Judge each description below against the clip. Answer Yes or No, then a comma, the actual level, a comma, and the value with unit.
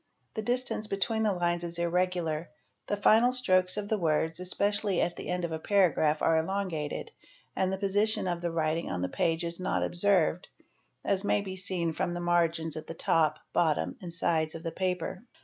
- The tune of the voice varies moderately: Yes, average, 3.2 semitones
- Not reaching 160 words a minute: No, average, 200 wpm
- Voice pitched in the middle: Yes, medium, 175 Hz